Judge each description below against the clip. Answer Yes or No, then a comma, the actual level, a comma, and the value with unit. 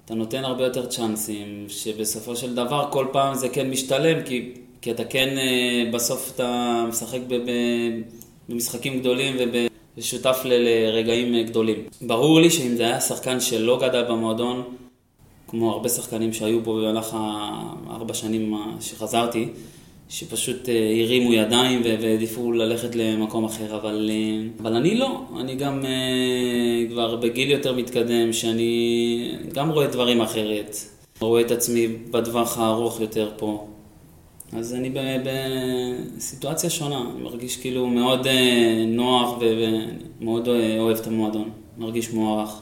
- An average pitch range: No, narrow, 1.9 semitones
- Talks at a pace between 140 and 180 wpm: No, average, 125 wpm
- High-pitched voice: No, low, 120 Hz